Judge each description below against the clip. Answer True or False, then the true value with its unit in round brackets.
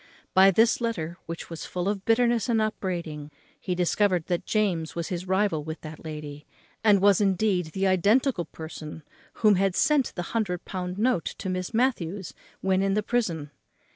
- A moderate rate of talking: True (170 wpm)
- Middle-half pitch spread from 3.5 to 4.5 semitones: True (4.0 semitones)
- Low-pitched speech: False (185 Hz)